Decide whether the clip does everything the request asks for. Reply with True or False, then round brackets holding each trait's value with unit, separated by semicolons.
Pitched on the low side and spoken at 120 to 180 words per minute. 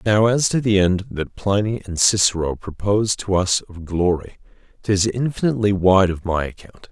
True (100 Hz; 175 wpm)